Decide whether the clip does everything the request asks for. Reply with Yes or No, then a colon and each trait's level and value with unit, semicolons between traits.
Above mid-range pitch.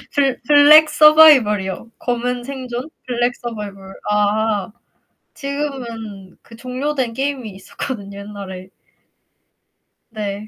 Yes: high, 235 Hz